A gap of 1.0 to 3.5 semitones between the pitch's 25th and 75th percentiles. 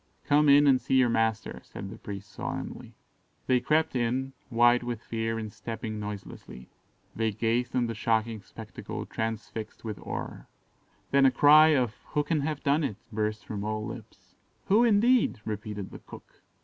No: average, 4.3 semitones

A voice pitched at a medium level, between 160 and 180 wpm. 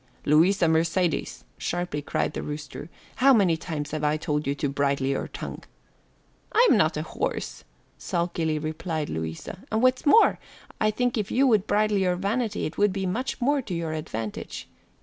Yes: medium, 175 Hz; average, 170 wpm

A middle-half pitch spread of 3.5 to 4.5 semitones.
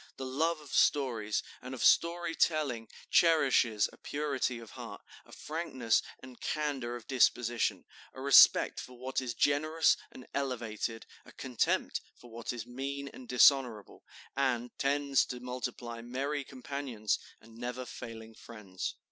No: average, 3.1 semitones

